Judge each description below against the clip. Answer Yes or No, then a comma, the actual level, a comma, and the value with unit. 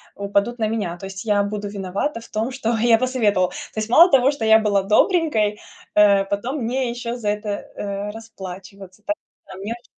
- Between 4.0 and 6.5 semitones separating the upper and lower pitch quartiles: No, average, 2.9 semitones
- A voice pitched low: No, high, 215 Hz